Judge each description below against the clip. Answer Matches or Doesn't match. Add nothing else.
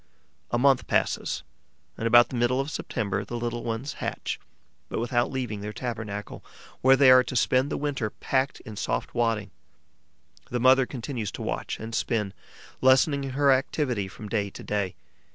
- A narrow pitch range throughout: Doesn't match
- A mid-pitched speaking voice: Doesn't match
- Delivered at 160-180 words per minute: Matches